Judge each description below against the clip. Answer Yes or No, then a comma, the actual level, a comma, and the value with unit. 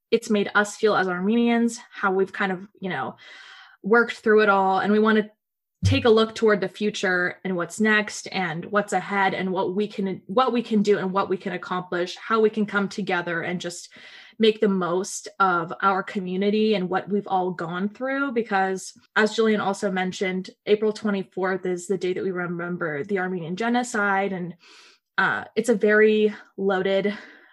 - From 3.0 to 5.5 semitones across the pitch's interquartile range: No, narrow, 2.4 semitones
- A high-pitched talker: Yes, high, 200 Hz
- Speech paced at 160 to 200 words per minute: Yes, average, 185 wpm